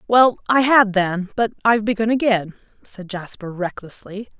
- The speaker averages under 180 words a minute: Yes, average, 150 wpm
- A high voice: Yes, high, 210 Hz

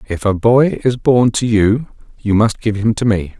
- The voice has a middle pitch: No, low, 110 Hz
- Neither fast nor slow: No, fast, 230 wpm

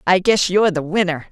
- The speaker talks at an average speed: No, fast, 230 wpm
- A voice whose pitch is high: No, medium, 180 Hz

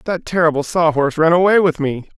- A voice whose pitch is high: No, medium, 165 Hz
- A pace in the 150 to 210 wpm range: No, fast, 220 wpm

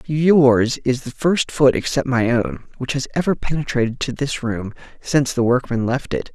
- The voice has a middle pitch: No, low, 130 Hz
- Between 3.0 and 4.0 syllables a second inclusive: No, 4.7 syllables/s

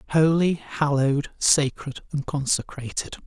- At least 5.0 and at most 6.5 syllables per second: No, 4.2 syllables/s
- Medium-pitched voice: Yes, medium, 145 Hz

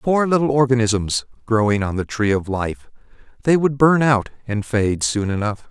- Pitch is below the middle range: Yes, low, 120 Hz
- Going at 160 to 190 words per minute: Yes, average, 170 wpm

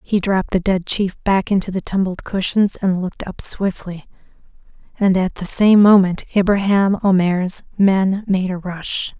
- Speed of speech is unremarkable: Yes, average, 165 wpm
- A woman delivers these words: Yes, female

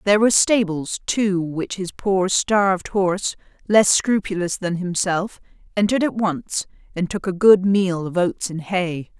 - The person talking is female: Yes, female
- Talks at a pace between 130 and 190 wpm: Yes, average, 165 wpm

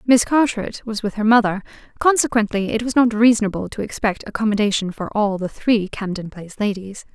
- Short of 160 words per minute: No, average, 175 wpm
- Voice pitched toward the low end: No, high, 215 Hz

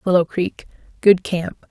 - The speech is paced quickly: No, slow, 105 wpm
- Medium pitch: Yes, medium, 180 Hz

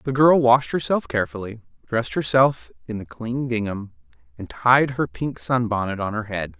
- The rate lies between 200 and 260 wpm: No, average, 175 wpm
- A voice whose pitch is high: No, low, 115 Hz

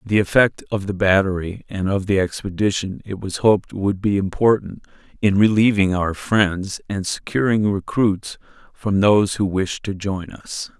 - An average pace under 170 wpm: Yes, average, 160 wpm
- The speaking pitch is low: Yes, low, 100 Hz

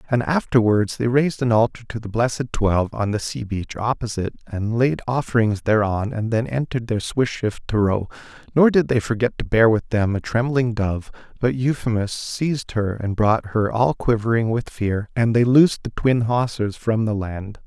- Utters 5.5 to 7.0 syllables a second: No, 5.1 syllables/s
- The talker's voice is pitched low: Yes, low, 115 Hz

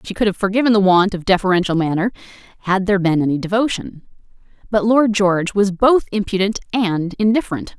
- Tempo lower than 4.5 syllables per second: No, 6.1 syllables/s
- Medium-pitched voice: No, high, 195 Hz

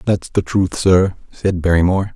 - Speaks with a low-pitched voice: Yes, very low, 90 Hz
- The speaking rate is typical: Yes, average, 165 wpm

